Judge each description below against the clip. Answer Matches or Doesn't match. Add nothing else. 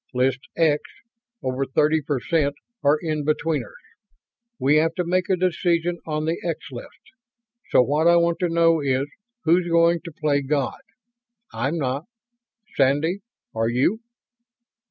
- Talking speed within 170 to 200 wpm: Doesn't match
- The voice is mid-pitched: Matches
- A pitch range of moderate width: Matches